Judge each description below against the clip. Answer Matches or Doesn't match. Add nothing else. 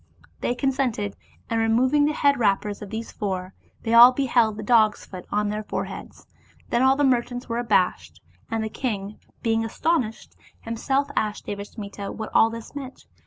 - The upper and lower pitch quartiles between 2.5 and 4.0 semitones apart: Matches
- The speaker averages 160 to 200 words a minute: Matches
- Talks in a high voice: Matches